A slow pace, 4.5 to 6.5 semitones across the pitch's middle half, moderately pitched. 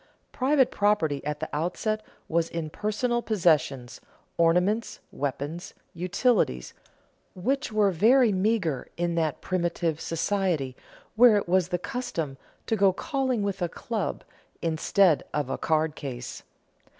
Yes: slow, 125 wpm; average, 5.3 semitones; medium, 180 Hz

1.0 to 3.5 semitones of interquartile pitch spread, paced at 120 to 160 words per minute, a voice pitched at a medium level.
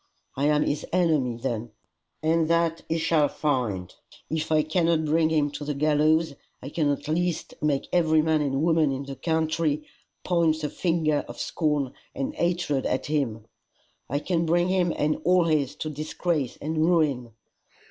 No: narrow, 2.4 semitones; average, 170 wpm; medium, 155 Hz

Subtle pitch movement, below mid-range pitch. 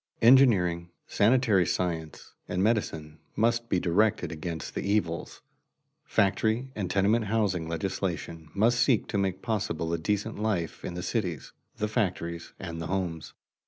No: average, 4.5 semitones; very low, 95 Hz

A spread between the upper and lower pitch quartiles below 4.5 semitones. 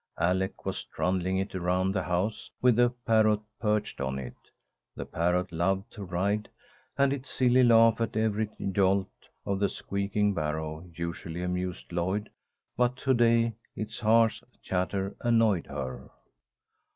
Yes: average, 3.9 semitones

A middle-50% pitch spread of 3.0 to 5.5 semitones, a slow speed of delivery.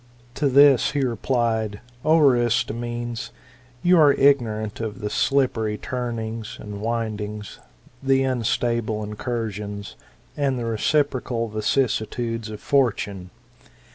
Yes: average, 3.5 semitones; slow, 105 wpm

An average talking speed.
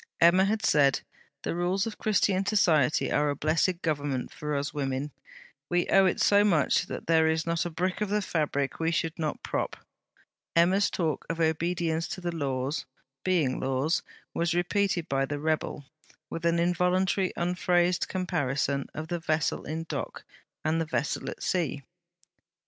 Yes: average, 165 wpm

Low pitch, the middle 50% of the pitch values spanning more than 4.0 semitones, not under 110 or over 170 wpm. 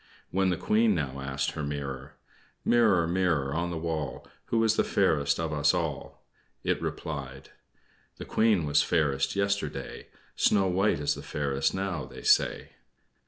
Yes: very low, 80 Hz; average, 5.3 semitones; average, 155 wpm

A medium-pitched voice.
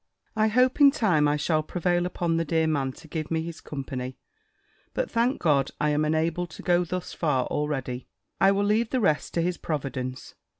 Yes: medium, 160 Hz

